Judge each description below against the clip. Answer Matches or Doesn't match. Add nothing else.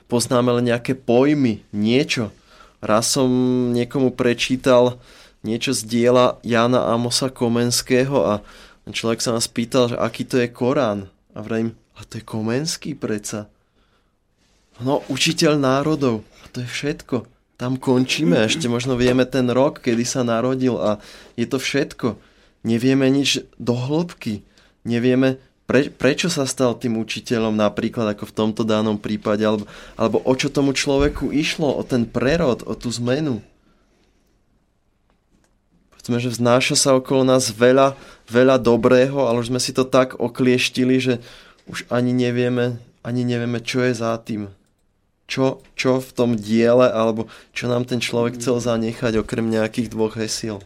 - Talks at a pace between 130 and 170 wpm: Matches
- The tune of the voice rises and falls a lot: Doesn't match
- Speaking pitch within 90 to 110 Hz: Doesn't match